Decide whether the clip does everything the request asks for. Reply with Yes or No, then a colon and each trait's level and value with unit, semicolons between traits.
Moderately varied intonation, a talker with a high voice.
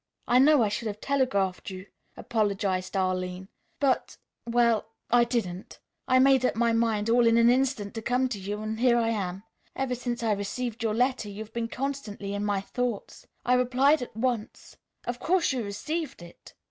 Yes: average, 3.6 semitones; high, 230 Hz